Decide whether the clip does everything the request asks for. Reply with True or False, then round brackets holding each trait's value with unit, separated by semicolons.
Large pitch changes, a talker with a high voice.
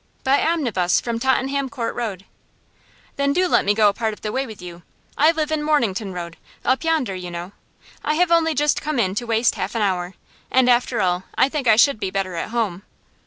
True (6.4 semitones; 235 Hz)